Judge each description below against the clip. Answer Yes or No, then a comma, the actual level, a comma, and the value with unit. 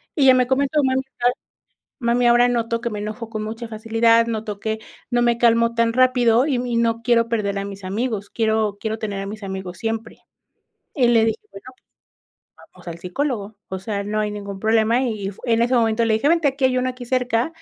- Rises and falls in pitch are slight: Yes, narrow, 2.3 semitones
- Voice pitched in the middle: No, high, 230 Hz